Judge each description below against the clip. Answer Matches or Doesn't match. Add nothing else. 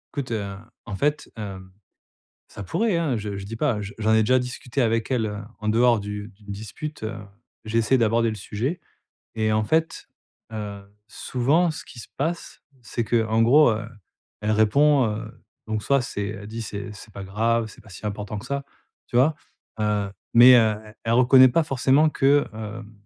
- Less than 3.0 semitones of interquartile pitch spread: Doesn't match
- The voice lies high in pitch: Doesn't match